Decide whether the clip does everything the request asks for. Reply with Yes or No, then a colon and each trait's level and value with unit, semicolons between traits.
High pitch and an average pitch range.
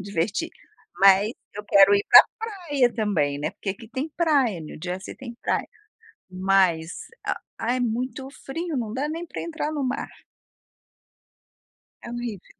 No: high, 230 Hz; wide, 6.3 semitones